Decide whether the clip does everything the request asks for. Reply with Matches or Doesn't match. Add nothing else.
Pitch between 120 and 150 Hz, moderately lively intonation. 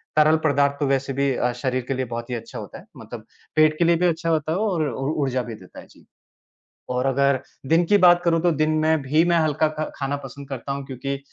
Matches